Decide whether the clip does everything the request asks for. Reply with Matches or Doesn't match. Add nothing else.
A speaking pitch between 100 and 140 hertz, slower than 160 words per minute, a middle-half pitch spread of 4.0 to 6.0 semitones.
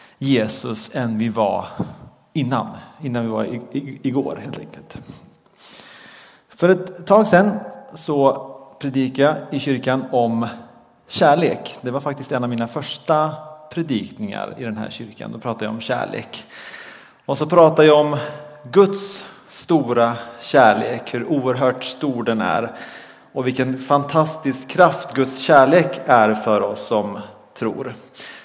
Matches